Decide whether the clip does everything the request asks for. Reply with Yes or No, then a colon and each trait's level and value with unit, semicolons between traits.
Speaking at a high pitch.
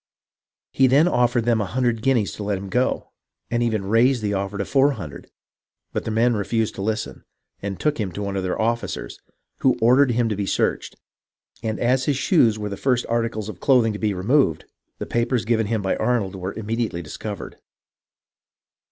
No: low, 110 Hz